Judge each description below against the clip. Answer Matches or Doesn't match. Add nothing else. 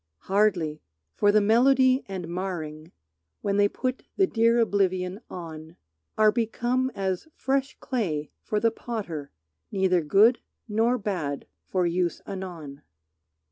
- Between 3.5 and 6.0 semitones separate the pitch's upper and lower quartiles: Matches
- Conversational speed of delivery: Doesn't match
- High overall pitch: Matches